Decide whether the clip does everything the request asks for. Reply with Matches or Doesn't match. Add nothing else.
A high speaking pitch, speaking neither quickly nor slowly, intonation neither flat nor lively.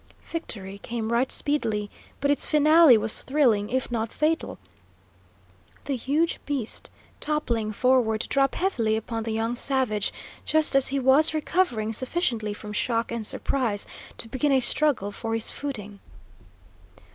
Matches